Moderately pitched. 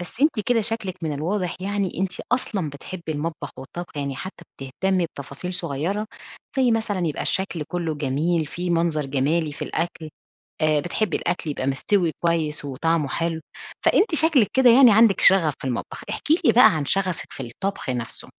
Yes: medium, 170 Hz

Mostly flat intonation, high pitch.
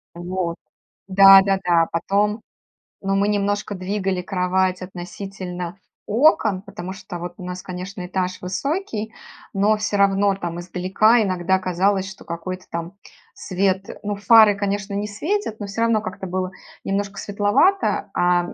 Yes: narrow, 2.0 semitones; high, 195 Hz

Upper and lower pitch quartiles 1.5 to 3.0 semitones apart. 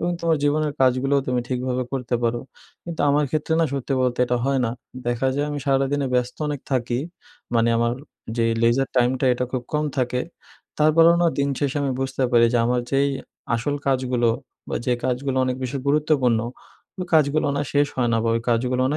Yes: narrow, 2.6 semitones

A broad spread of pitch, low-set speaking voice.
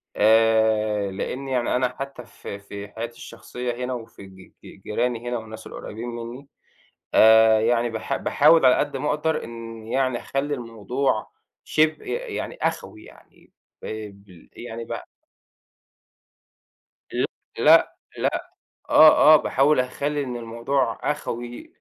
No: average, 3.4 semitones; low, 120 Hz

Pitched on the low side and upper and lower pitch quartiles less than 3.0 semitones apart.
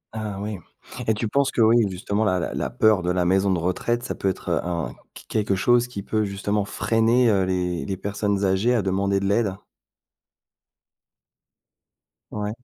Yes: low, 100 Hz; narrow, 2.6 semitones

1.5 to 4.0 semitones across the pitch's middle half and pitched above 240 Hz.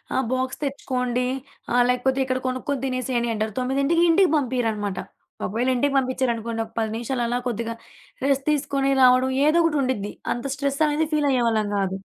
Yes: average, 2.8 semitones; very high, 255 Hz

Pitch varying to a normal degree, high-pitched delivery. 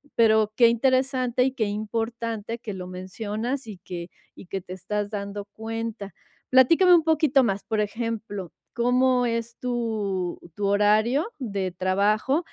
Yes: average, 3.4 semitones; high, 220 Hz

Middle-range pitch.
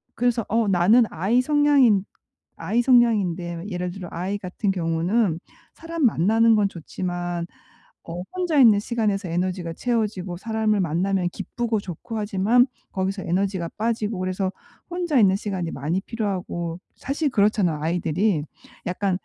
No: high, 195 Hz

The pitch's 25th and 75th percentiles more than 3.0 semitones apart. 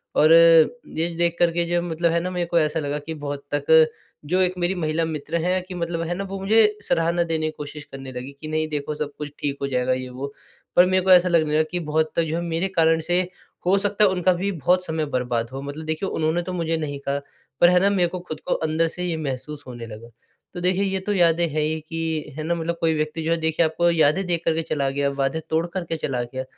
No: average, 2.7 semitones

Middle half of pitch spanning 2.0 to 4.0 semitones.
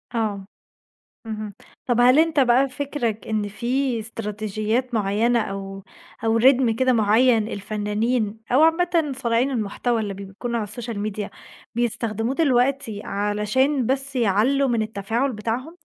Yes: average, 3.5 semitones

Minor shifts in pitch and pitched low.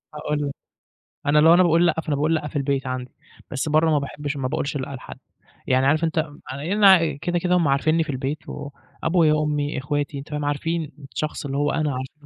No: narrow, 2.3 semitones; medium, 150 Hz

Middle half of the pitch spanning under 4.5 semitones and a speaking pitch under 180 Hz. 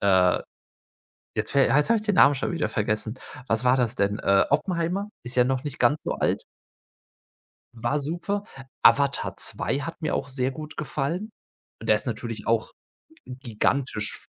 No: average, 4.8 semitones; low, 135 Hz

